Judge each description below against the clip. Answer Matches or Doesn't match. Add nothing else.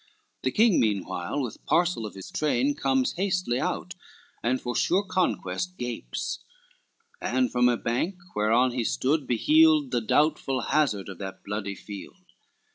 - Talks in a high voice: Doesn't match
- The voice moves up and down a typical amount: Doesn't match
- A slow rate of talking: Doesn't match